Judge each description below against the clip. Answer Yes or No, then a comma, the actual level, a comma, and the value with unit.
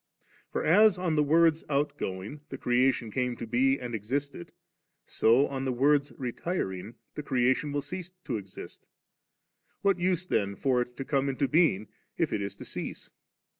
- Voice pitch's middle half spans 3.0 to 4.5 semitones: Yes, average, 3.8 semitones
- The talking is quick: No, average, 165 wpm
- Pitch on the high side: No, low, 135 Hz